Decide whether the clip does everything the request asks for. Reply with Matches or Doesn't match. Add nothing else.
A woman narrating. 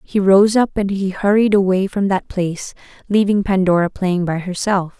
Matches